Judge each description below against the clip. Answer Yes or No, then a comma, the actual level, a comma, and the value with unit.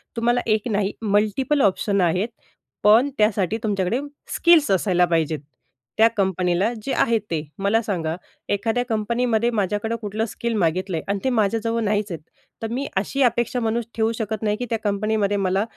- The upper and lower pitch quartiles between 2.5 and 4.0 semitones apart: Yes, average, 2.9 semitones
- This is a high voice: Yes, high, 210 Hz